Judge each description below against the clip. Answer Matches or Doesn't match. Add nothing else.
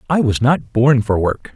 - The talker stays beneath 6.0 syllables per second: Matches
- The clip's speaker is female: Doesn't match